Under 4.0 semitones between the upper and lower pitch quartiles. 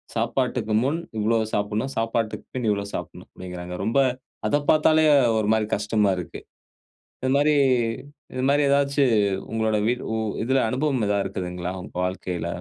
No: average, 4.6 semitones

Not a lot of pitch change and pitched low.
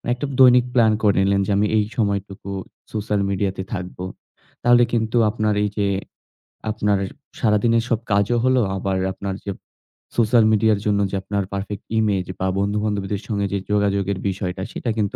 Yes: narrow, 2.0 semitones; low, 105 Hz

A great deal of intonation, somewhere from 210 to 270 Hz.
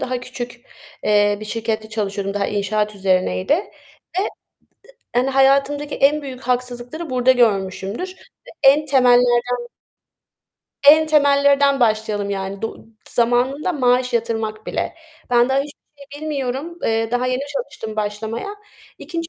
No: average, 4.3 semitones; high, 245 Hz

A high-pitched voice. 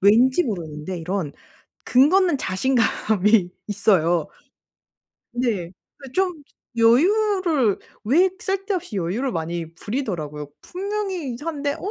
Yes: high, 240 Hz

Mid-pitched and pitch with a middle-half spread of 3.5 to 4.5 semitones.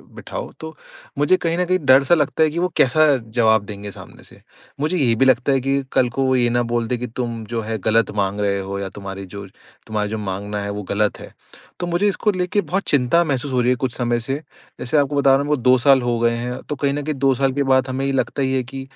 No: low, 130 Hz; average, 3.9 semitones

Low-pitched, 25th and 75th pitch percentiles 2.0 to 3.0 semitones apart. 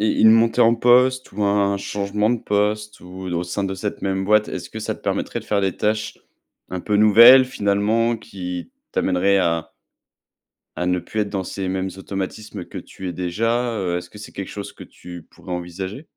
Yes: low, 100 Hz; narrow, 2.6 semitones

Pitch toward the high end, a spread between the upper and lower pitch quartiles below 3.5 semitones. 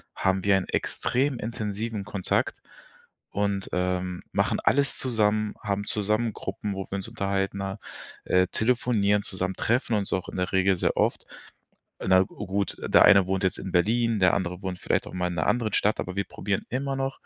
No: low, 100 Hz; average, 2.7 semitones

